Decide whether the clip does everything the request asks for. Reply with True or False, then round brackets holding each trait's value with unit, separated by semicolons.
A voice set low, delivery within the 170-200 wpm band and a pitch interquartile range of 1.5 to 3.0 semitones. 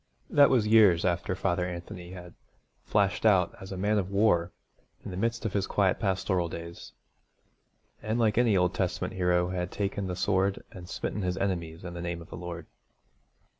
True (95 Hz; 185 wpm; 2.5 semitones)